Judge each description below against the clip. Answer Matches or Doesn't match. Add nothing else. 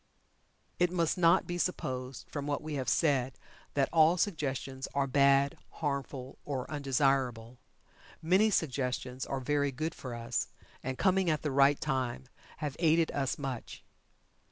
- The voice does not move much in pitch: Doesn't match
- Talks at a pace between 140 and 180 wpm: Matches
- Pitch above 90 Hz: Matches